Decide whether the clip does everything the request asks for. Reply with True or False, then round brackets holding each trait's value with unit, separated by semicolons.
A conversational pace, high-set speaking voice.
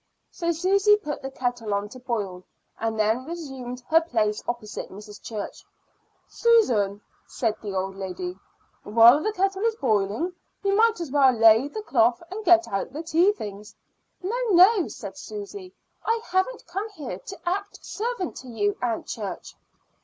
True (160 wpm; 265 Hz)